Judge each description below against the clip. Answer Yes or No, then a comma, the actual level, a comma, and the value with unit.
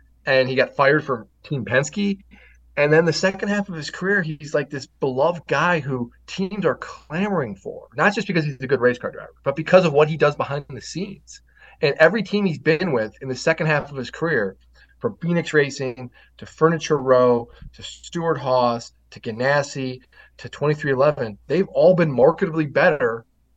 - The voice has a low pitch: No, medium, 150 Hz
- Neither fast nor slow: Yes, average, 190 wpm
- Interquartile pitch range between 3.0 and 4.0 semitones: No, average, 4.7 semitones